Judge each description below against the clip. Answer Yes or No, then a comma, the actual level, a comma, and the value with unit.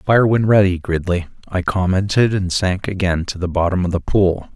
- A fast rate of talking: No, average, 195 wpm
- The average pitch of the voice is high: No, very low, 95 Hz